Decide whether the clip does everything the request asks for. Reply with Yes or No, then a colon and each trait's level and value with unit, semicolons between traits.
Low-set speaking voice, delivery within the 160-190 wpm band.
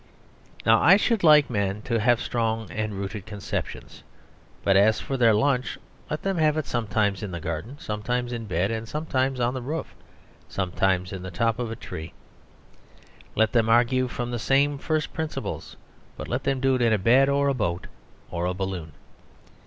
Yes: low, 115 Hz; average, 185 wpm